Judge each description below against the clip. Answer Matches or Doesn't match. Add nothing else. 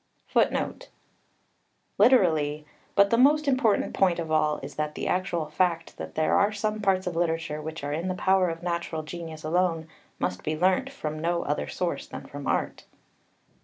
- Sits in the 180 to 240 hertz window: Doesn't match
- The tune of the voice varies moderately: Matches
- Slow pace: Doesn't match